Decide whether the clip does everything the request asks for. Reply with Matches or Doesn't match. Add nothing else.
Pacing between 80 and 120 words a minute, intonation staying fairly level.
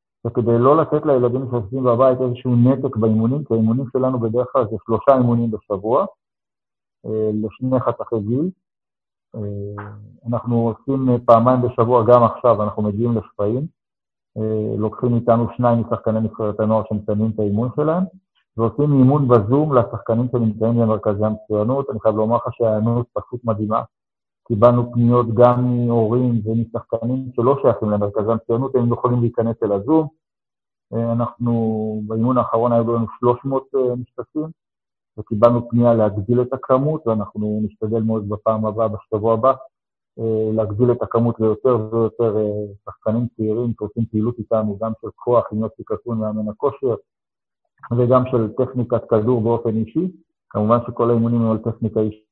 Doesn't match